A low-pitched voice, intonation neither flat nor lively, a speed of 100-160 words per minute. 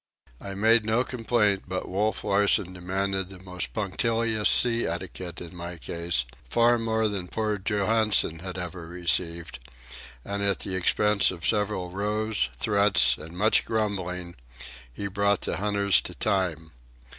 Yes: low, 100 Hz; average, 3.2 semitones; average, 140 wpm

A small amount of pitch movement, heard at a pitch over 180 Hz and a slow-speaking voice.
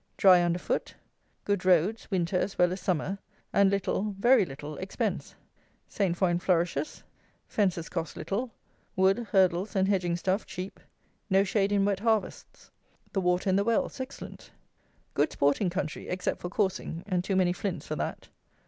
No: narrow, 2.2 semitones; high, 190 Hz; average, 160 wpm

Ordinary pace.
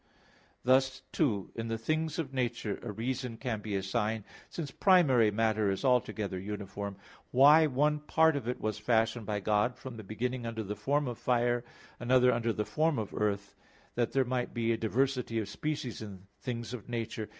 Yes: average, 185 wpm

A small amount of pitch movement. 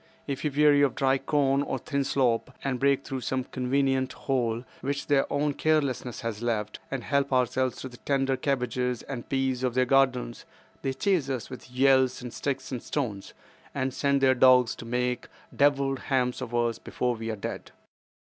Yes: narrow, 1.8 semitones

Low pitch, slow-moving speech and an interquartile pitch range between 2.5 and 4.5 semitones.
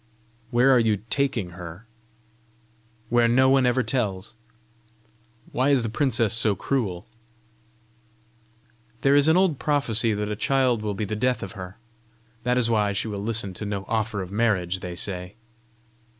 No: low, 110 Hz; average, 160 wpm; average, 4.2 semitones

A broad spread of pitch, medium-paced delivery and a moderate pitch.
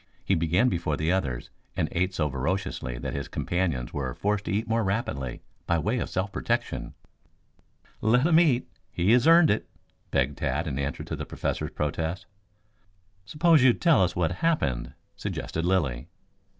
No: wide, 7.5 semitones; average, 165 wpm; very low, 90 Hz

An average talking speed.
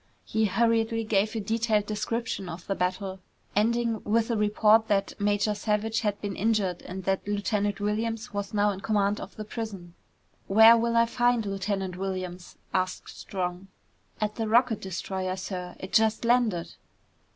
Yes: average, 160 wpm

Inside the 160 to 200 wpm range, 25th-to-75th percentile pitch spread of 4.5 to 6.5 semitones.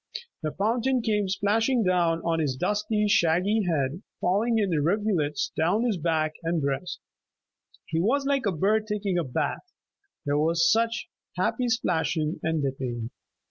No: average, 145 wpm; average, 5.3 semitones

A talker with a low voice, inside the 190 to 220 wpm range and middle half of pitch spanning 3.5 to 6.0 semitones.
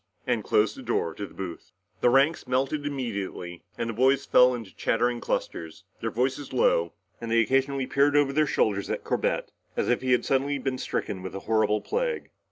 Yes: low, 125 Hz; average, 195 wpm; average, 4.5 semitones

